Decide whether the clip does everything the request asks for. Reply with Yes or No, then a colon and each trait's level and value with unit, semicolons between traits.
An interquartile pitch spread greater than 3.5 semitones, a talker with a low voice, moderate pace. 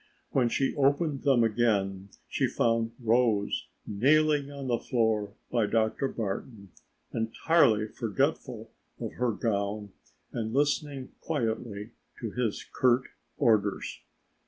No: average, 4.0 semitones; low, 115 Hz; slow, 110 wpm